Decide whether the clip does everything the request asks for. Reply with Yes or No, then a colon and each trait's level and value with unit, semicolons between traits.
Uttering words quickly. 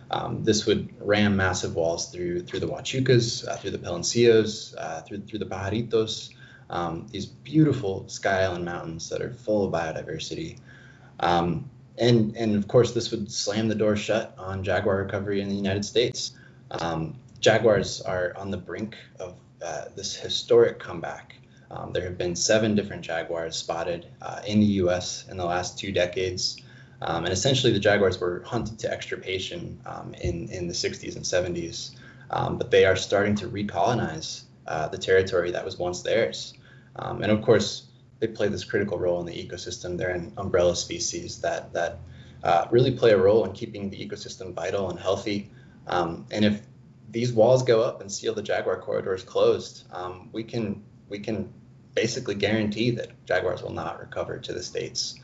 No: average, 180 wpm